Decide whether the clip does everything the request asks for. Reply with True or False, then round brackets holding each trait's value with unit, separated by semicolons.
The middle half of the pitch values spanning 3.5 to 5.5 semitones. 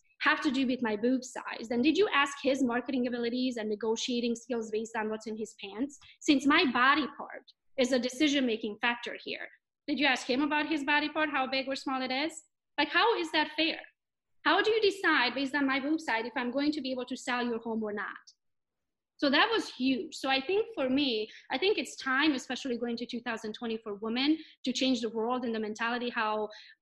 True (3.9 semitones)